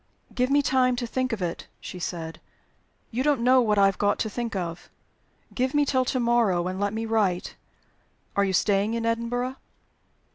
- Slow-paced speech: No, average, 190 wpm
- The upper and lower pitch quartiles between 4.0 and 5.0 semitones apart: Yes, average, 4.4 semitones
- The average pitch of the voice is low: No, high, 230 Hz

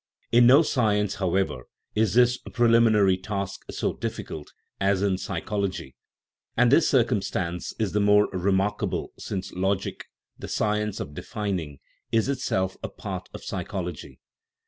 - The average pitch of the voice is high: No, low, 100 Hz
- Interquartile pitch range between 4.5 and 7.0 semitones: No, average, 2.9 semitones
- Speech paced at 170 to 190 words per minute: No, average, 140 wpm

